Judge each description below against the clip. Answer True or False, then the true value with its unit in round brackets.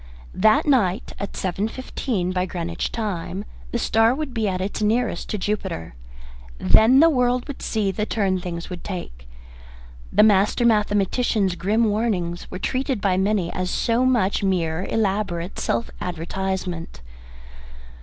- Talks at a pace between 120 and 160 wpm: True (145 wpm)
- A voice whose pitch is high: True (200 Hz)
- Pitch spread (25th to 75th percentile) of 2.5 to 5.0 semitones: True (3.7 semitones)